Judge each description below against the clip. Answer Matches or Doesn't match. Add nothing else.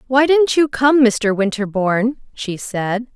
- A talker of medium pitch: Doesn't match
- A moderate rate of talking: Matches